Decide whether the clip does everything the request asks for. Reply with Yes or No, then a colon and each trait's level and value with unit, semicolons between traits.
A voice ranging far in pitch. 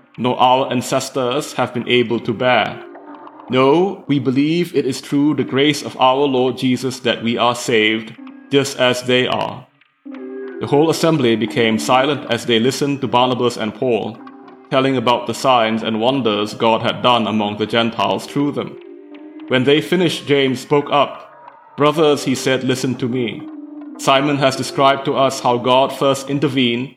No: average, 2.8 semitones